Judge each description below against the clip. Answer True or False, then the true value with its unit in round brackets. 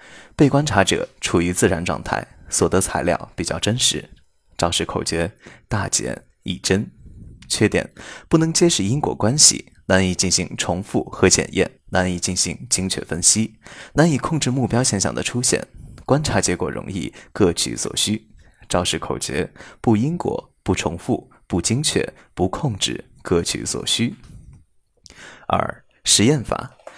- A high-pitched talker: False (95 Hz)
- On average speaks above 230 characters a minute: False (220 characters per minute)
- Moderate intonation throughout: False (6.3 semitones)